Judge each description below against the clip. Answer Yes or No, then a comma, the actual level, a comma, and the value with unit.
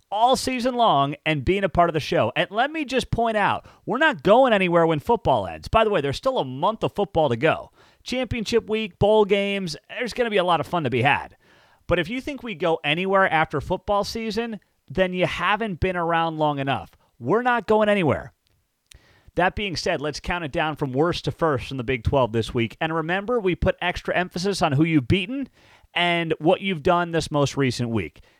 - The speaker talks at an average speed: No, fast, 220 wpm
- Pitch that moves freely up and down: Yes, wide, 5.8 semitones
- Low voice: No, medium, 175 Hz